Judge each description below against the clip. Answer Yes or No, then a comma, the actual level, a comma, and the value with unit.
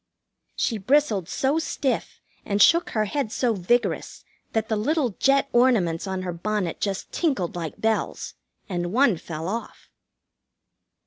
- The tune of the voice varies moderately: No, wide, 6.0 semitones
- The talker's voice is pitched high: Yes, high, 215 Hz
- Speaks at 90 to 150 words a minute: Yes, average, 140 wpm